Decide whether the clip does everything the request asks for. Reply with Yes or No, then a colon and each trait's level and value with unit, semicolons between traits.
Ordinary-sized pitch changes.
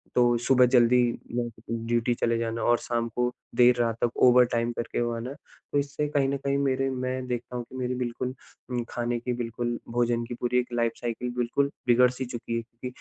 No: narrow, 1.2 semitones